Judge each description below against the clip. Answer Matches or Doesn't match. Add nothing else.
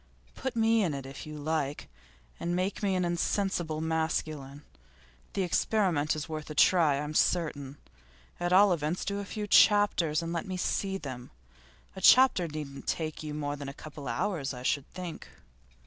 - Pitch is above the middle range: Doesn't match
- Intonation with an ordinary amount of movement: Matches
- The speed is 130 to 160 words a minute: Doesn't match